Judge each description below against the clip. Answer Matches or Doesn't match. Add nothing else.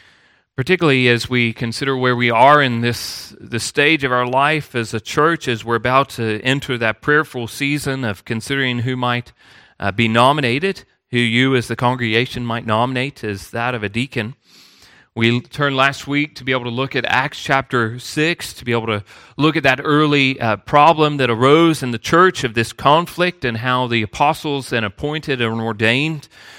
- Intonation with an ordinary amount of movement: Matches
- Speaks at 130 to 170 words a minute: Doesn't match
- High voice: Doesn't match